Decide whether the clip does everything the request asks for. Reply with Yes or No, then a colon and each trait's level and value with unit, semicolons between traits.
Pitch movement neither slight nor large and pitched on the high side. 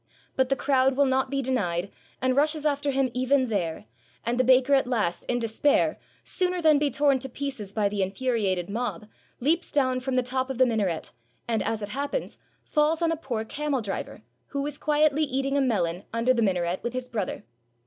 Yes: average, 4.3 semitones; very high, 255 Hz